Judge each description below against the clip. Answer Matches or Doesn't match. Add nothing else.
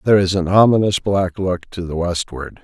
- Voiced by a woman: Doesn't match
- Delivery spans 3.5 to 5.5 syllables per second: Matches